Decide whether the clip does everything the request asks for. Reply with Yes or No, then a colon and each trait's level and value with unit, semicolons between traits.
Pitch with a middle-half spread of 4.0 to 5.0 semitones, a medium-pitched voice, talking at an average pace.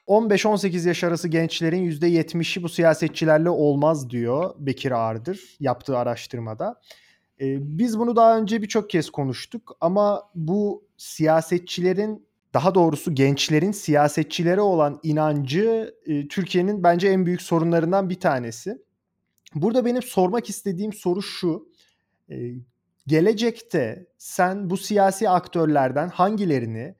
Yes: average, 4.4 semitones; medium, 175 Hz; average, 115 wpm